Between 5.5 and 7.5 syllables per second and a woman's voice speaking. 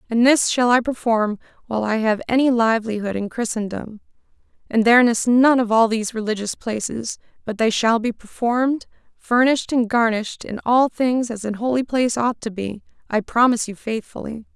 Yes: 5.6 syllables/s; female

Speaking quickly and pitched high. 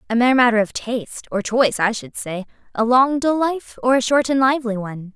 Yes: fast, 220 wpm; high, 240 Hz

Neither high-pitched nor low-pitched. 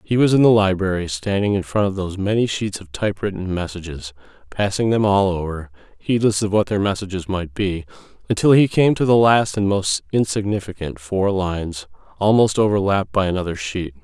No: very low, 95 Hz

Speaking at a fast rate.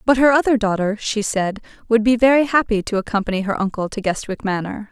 Yes: fast, 210 wpm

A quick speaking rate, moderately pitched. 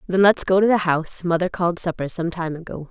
Yes: fast, 250 wpm; medium, 175 Hz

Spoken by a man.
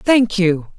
No: female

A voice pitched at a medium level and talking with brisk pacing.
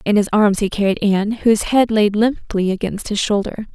No: high, 210 Hz; fast, 210 wpm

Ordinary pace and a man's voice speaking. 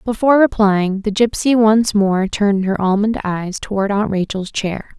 No: average, 170 wpm; female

